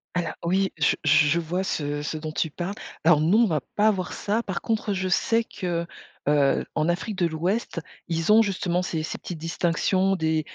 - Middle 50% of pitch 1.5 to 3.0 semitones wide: No, average, 3.4 semitones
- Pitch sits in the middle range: Yes, medium, 175 Hz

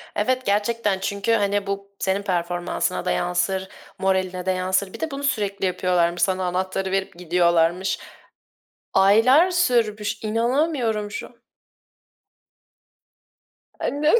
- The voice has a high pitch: Yes, high, 200 Hz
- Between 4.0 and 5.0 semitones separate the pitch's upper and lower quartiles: No, average, 3.5 semitones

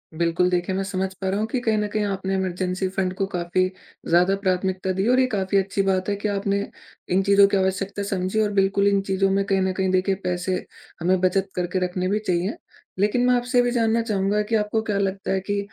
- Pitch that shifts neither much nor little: No, narrow, 1.5 semitones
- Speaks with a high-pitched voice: Yes, high, 195 Hz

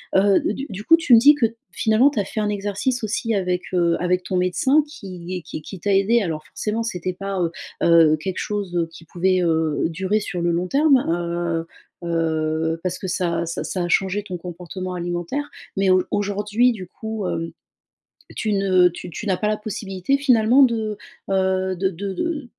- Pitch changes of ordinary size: Yes, average, 3.6 semitones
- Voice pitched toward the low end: No, high, 190 Hz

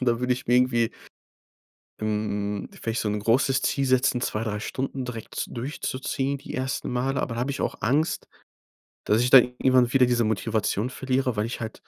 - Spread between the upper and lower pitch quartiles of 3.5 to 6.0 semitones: No, narrow, 2.6 semitones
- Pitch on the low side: Yes, low, 125 Hz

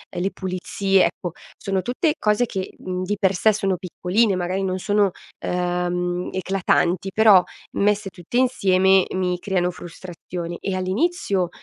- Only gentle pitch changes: Yes, narrow, 2.1 semitones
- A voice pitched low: No, high, 190 Hz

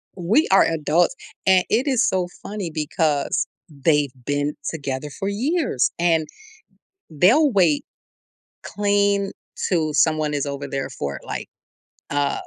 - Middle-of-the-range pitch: Yes, medium, 165 Hz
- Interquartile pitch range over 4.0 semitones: Yes, wide, 5.6 semitones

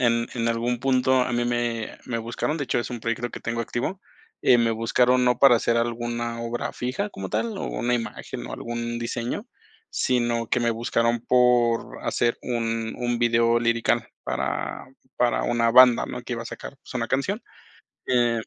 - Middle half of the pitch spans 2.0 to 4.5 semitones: No, narrow, 1.0 semitones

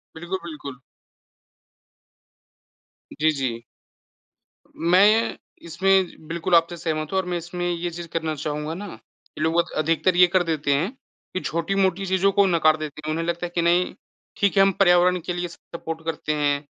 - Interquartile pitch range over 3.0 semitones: No, narrow, 2.6 semitones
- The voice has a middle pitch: Yes, medium, 170 Hz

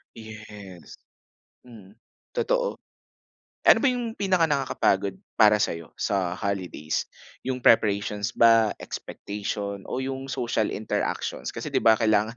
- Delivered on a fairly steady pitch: No, average, 4.5 semitones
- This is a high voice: No, low, 110 Hz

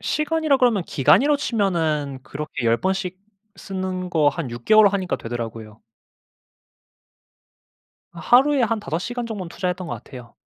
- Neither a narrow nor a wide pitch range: No, wide, 7.4 semitones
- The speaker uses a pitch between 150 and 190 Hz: Yes, medium, 185 Hz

